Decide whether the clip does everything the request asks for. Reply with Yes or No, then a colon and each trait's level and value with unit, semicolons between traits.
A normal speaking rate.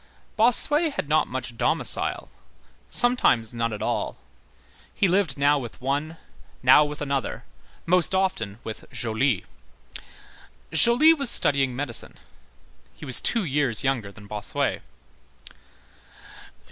No: slow, 115 wpm